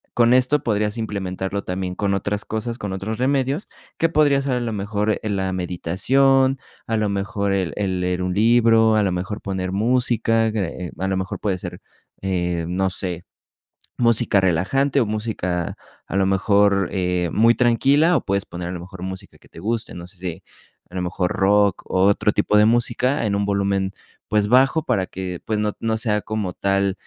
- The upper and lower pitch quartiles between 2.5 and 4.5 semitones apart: Yes, average, 3.4 semitones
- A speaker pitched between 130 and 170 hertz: No, low, 100 Hz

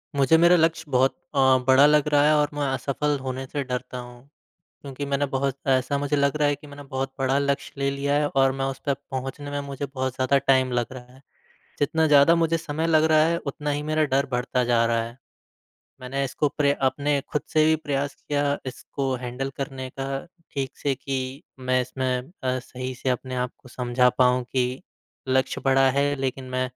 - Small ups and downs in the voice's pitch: Yes, narrow, 2.0 semitones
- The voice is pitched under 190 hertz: Yes, low, 135 Hz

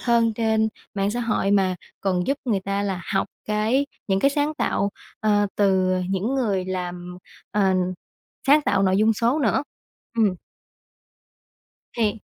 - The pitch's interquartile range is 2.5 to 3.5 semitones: Yes, average, 3.2 semitones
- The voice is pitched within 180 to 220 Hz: Yes, high, 205 Hz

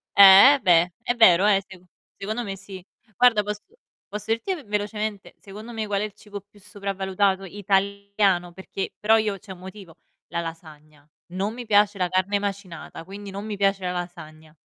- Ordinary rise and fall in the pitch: No, narrow, 2.2 semitones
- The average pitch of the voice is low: No, high, 200 Hz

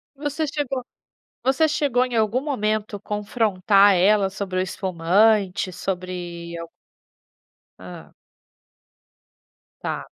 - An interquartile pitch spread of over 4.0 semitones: Yes, average, 5.2 semitones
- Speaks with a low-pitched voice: No, high, 205 Hz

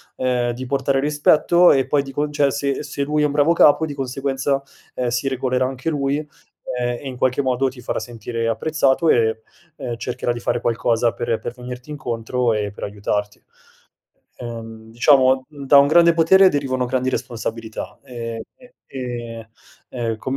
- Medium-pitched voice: No, low, 130 Hz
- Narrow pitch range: No, average, 3.0 semitones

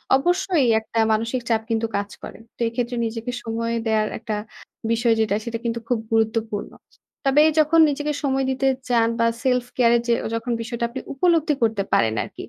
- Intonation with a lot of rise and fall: No, average, 2.9 semitones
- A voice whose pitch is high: Yes, high, 235 Hz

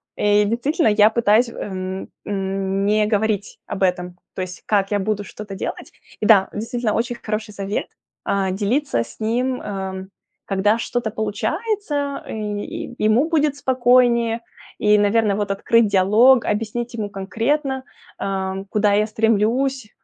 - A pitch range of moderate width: Yes, average, 3.2 semitones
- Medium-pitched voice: No, high, 215 Hz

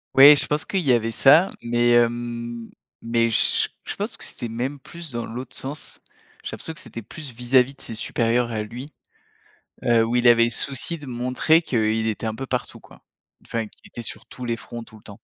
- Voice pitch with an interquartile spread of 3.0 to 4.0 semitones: No, narrow, 2.5 semitones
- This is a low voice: Yes, low, 120 Hz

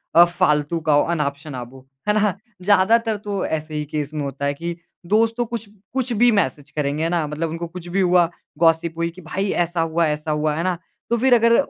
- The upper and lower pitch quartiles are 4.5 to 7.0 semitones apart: Yes, average, 4.8 semitones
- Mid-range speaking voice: Yes, medium, 170 Hz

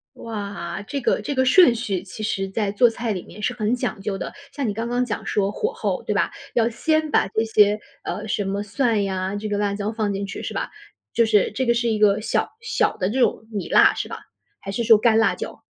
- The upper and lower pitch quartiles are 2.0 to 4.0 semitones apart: Yes, average, 2.8 semitones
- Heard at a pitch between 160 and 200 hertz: No, high, 215 Hz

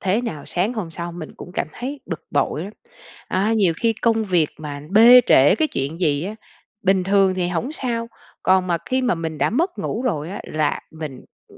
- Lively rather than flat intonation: Yes, wide, 5.9 semitones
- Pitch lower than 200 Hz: Yes, medium, 185 Hz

